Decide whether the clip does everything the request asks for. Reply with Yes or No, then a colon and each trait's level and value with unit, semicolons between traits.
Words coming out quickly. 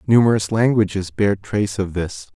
No: average, 150 wpm